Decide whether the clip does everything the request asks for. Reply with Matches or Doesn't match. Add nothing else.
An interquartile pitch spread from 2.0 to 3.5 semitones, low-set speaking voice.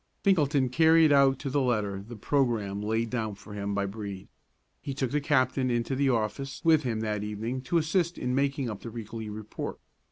Doesn't match